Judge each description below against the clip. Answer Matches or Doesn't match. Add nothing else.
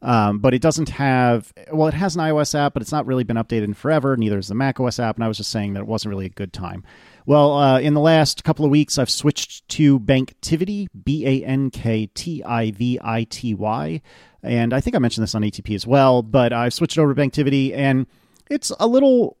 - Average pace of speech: Doesn't match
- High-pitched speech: Doesn't match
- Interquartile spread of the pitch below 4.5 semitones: Doesn't match